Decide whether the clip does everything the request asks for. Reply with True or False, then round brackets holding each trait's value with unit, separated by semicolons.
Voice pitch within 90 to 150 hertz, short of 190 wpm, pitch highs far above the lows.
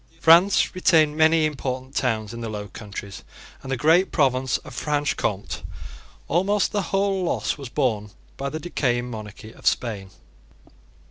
True (135 Hz; 150 wpm; 6.3 semitones)